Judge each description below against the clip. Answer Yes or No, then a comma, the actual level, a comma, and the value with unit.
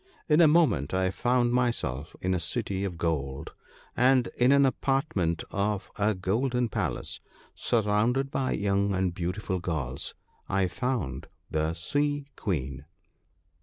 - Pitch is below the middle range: Yes, low, 100 Hz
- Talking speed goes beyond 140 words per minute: No, slow, 135 wpm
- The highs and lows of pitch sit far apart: Yes, wide, 6.6 semitones